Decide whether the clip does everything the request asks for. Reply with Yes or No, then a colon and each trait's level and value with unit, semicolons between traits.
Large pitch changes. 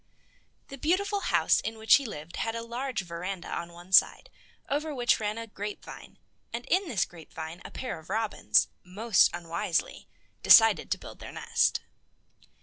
Yes: wide, 6.2 semitones